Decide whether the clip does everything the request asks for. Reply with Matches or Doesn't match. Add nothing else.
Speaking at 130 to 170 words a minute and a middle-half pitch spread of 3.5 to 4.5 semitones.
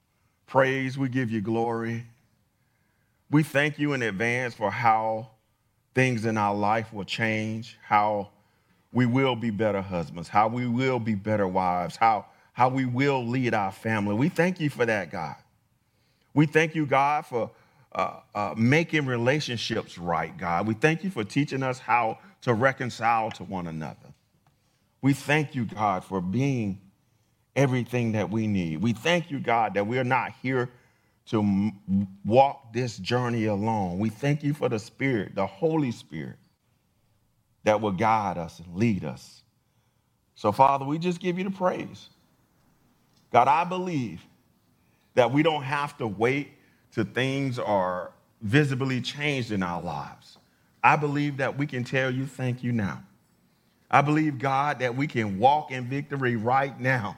Matches